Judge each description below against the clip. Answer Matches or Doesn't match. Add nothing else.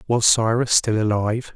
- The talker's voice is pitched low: Matches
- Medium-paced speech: Matches